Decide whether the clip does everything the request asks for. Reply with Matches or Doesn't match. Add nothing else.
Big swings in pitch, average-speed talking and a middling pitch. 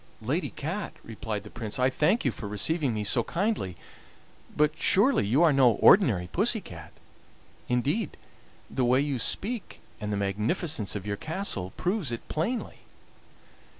Doesn't match